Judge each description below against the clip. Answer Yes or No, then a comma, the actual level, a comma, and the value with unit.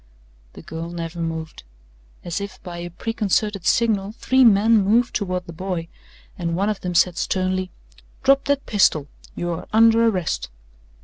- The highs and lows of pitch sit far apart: No, average, 4.2 semitones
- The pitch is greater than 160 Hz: Yes, medium, 185 Hz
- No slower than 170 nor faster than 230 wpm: No, average, 160 wpm